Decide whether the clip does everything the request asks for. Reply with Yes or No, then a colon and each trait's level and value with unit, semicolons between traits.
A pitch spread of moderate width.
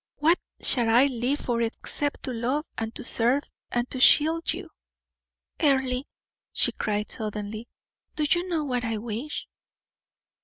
Yes: average, 4.2 semitones